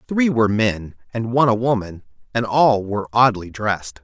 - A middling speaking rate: Yes, average, 180 wpm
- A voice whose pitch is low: Yes, low, 110 Hz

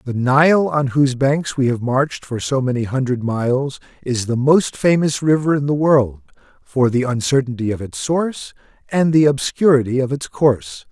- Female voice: No, male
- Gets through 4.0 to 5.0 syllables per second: Yes, 4.9 syllables/s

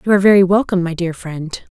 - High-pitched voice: No, medium, 180 Hz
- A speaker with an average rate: No, fast, 240 wpm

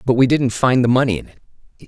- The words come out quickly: Yes, fast, 255 wpm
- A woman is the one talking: No, male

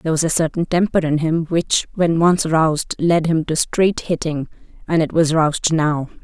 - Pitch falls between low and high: Yes, medium, 160 Hz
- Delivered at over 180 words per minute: Yes, average, 200 wpm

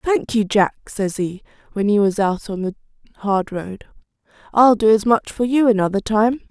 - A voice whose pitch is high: Yes, high, 215 Hz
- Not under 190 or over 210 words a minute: Yes, average, 195 wpm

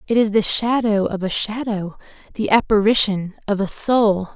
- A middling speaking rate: Yes, average, 165 wpm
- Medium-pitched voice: No, high, 210 Hz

